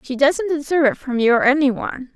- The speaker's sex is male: No, female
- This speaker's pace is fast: Yes, fast, 250 wpm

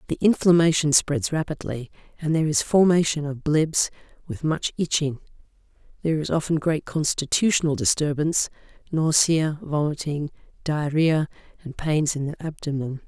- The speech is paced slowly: Yes, slow, 125 wpm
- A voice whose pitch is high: No, medium, 155 Hz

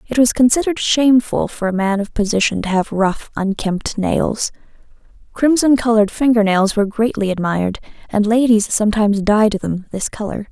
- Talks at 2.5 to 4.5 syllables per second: No, 5.4 syllables/s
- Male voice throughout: No, female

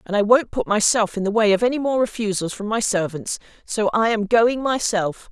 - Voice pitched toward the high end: Yes, high, 215 Hz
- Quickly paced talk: Yes, fast, 225 wpm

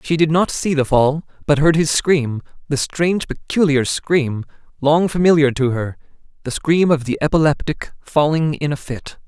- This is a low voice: No, medium, 150 Hz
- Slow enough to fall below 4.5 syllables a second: No, 4.7 syllables/s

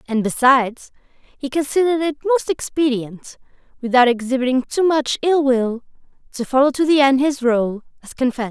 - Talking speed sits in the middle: Yes, average, 155 wpm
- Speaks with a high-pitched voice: Yes, very high, 265 Hz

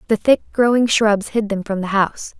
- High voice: Yes, high, 215 Hz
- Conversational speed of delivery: No, fast, 225 wpm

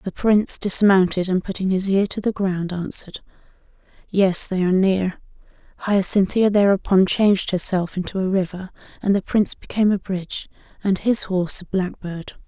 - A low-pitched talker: No, high, 190 Hz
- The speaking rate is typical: Yes, average, 160 wpm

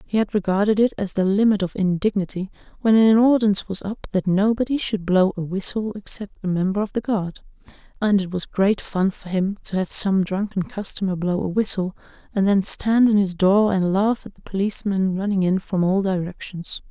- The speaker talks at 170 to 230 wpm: Yes, average, 200 wpm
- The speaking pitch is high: Yes, high, 195 Hz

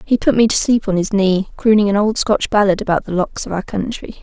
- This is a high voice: Yes, high, 205 Hz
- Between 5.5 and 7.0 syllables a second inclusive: Yes, 5.7 syllables/s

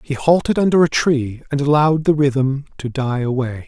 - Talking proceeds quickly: No, average, 195 wpm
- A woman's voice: No, male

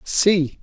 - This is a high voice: No, medium, 175 Hz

